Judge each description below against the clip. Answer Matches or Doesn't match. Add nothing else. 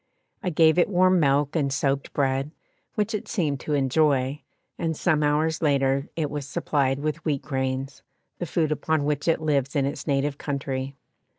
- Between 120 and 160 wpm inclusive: Doesn't match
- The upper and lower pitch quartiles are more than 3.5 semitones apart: Doesn't match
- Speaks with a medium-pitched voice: Matches